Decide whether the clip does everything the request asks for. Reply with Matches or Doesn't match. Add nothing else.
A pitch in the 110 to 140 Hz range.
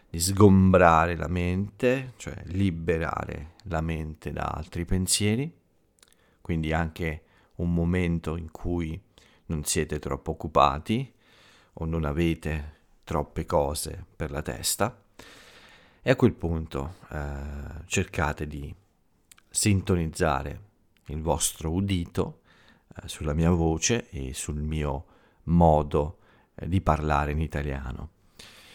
Doesn't match